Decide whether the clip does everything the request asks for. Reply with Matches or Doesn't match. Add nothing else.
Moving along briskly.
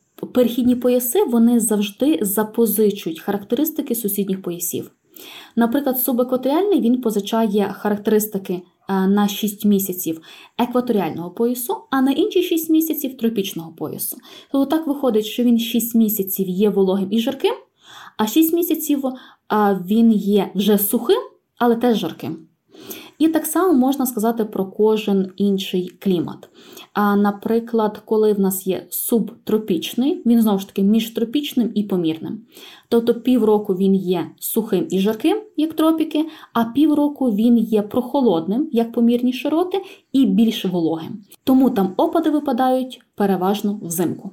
Doesn't match